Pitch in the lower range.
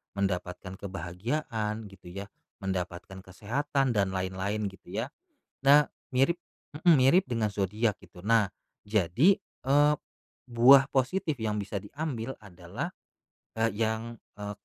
Yes: low, 110 Hz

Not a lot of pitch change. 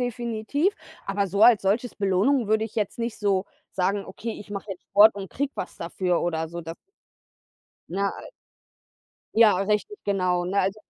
No: average, 3.1 semitones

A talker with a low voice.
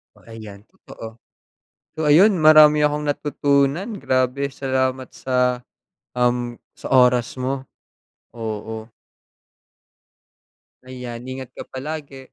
Yes: low, 130 Hz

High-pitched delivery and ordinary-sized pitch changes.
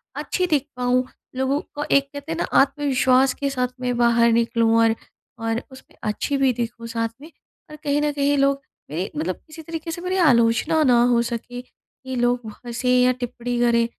Yes: very high, 250 Hz; average, 3.3 semitones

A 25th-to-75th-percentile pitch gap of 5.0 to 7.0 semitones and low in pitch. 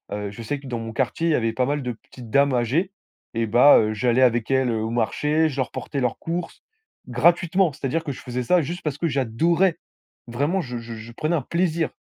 Yes: wide, 5.4 semitones; low, 130 Hz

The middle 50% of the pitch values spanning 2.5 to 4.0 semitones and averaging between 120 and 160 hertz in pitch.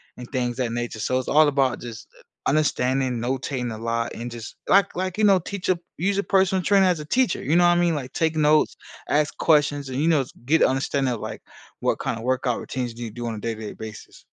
No: wide, 5.5 semitones; low, 135 Hz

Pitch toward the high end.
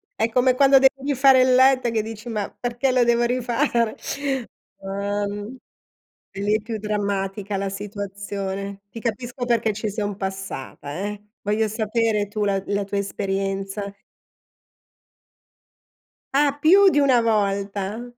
Yes: high, 210 Hz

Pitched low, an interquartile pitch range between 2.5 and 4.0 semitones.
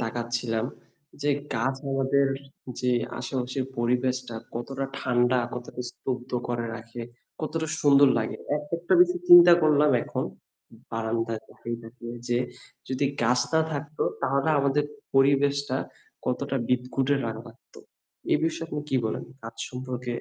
Yes: low, 130 Hz; average, 2.9 semitones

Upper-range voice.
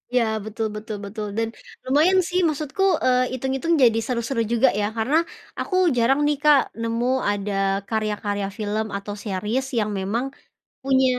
Yes: high, 235 Hz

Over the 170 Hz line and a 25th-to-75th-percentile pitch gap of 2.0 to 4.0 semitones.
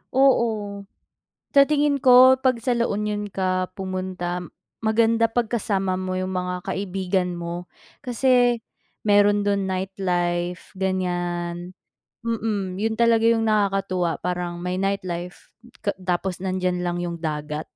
Yes: high, 190 Hz; average, 3.6 semitones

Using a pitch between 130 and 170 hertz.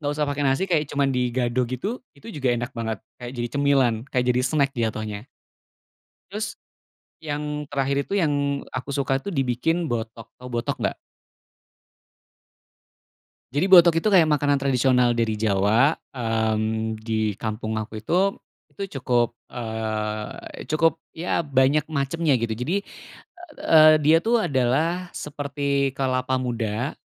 Yes: low, 135 Hz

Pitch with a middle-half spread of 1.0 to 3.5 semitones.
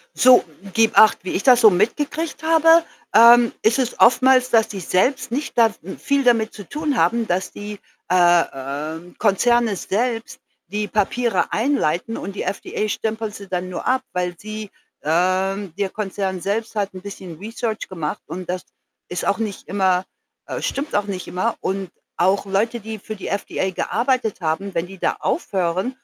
No: average, 4.1 semitones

